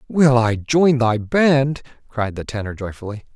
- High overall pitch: No, low, 125 Hz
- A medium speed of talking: Yes, average, 160 wpm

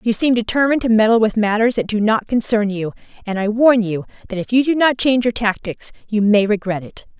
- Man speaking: No, female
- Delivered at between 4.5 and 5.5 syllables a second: No, 5.9 syllables/s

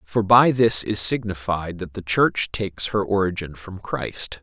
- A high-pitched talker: No, very low, 95 Hz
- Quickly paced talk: No, average, 175 wpm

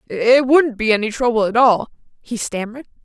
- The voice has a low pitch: No, high, 235 Hz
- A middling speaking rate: Yes, average, 180 wpm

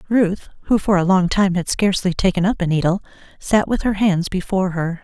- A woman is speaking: Yes, female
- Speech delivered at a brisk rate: Yes, fast, 215 wpm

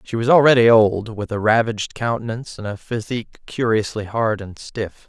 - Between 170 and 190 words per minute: Yes, average, 175 wpm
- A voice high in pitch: No, low, 110 Hz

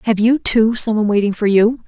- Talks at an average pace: No, fast, 255 wpm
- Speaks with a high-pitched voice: Yes, high, 220 Hz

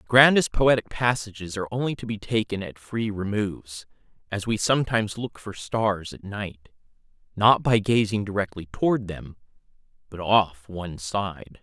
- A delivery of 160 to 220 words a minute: No, average, 150 wpm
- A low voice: Yes, low, 105 Hz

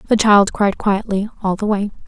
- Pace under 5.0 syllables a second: Yes, 4.6 syllables/s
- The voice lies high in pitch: Yes, high, 205 Hz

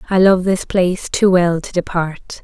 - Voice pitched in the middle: Yes, medium, 180 Hz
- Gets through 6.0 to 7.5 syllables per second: No, 4.5 syllables/s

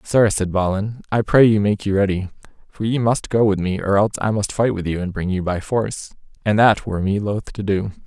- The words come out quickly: Yes, fast, 255 wpm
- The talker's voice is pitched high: No, low, 100 Hz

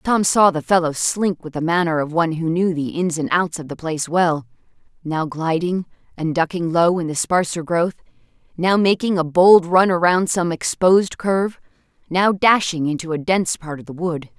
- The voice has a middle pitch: Yes, medium, 170 Hz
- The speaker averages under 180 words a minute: No, average, 190 wpm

